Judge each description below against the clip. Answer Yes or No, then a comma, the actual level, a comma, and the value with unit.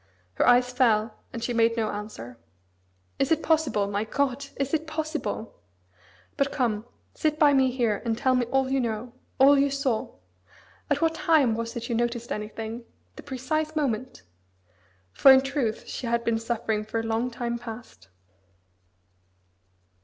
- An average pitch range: Yes, average, 3.5 semitones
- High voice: Yes, high, 240 Hz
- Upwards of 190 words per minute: No, average, 160 wpm